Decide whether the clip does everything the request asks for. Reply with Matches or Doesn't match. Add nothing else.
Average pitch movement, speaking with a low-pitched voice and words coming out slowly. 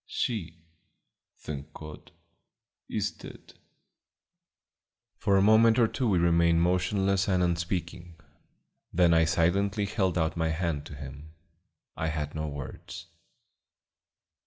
Matches